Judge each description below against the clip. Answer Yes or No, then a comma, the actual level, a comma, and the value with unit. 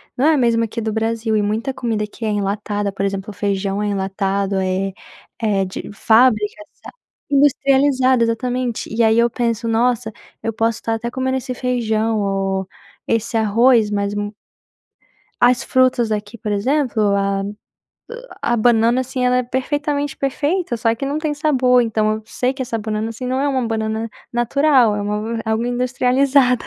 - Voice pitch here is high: Yes, high, 230 Hz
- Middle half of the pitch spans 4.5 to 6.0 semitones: No, average, 3.3 semitones